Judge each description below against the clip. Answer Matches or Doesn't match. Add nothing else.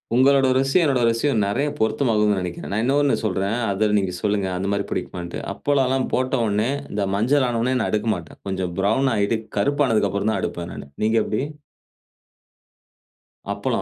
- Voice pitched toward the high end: Doesn't match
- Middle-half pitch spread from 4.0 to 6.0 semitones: Matches